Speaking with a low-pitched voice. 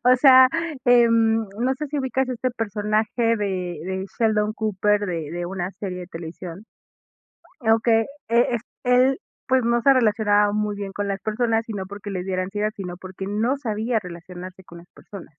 No: high, 210 Hz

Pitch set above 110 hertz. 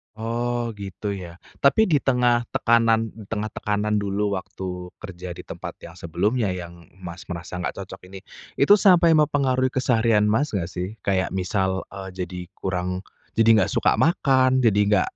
No: low, 105 Hz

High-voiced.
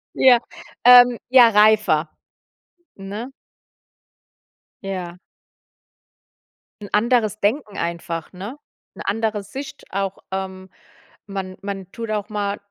Yes: high, 205 Hz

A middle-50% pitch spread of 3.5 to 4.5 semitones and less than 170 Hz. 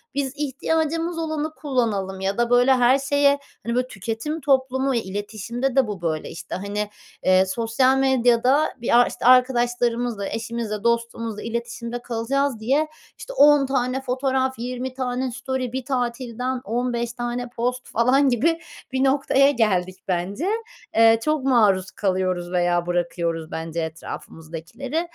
No: average, 3.8 semitones; high, 245 Hz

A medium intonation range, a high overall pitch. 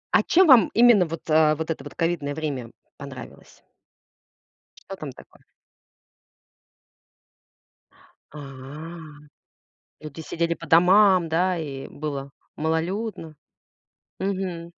No: average, 3.6 semitones; medium, 160 Hz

